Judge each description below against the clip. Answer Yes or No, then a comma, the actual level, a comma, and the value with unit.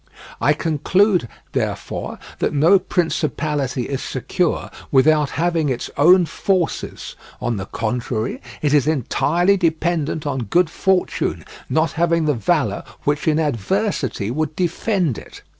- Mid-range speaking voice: Yes, medium, 155 Hz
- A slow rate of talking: Yes, slow, 125 wpm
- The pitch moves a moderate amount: Yes, average, 4.3 semitones